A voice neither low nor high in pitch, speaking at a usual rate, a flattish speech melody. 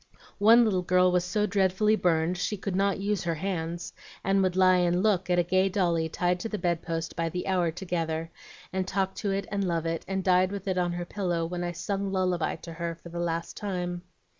No: medium, 180 Hz; fast, 225 wpm; narrow, 2.1 semitones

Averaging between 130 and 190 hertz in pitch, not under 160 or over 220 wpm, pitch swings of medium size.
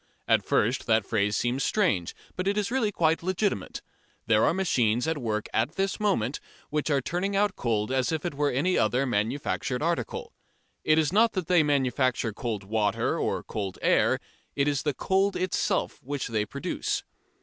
No: medium, 140 Hz; average, 180 wpm; wide, 7.8 semitones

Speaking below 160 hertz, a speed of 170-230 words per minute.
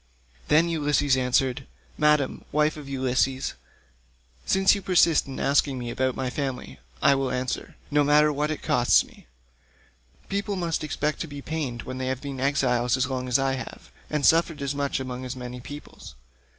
Yes: medium, 140 Hz; average, 175 wpm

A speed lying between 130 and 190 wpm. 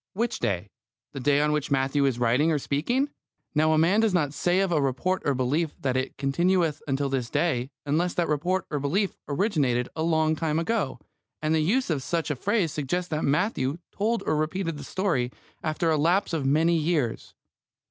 No: average, 200 wpm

